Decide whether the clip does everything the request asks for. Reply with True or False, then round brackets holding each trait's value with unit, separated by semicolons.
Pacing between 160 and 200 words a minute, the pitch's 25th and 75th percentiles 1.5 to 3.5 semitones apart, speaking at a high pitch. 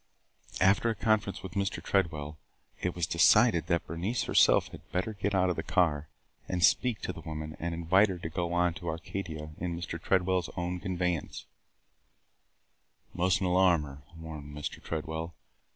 False (170 wpm; 2.6 semitones; 85 Hz)